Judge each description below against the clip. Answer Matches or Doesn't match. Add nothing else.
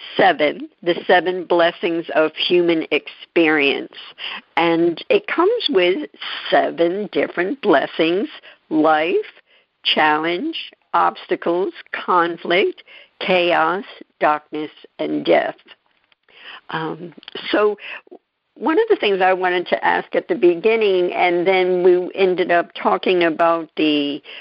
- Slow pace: Matches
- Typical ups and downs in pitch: Matches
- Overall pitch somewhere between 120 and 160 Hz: Doesn't match